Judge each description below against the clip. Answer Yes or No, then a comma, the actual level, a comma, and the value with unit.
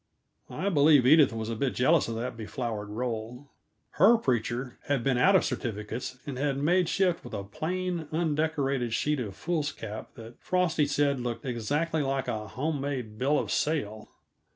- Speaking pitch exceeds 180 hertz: No, low, 135 Hz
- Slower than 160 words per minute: No, average, 170 wpm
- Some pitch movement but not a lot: Yes, average, 5.0 semitones